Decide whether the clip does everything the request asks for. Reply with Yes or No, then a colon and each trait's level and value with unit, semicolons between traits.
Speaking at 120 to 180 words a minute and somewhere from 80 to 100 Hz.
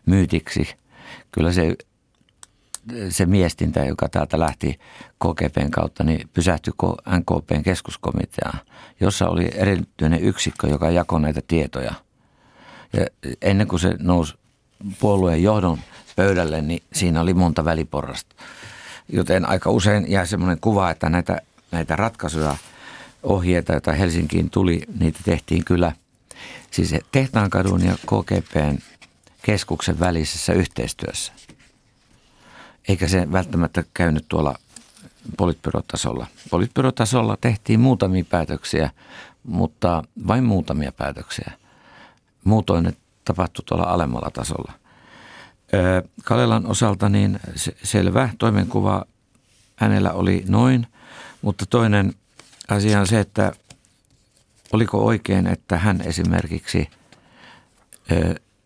No: average, 100 wpm; very low, 90 Hz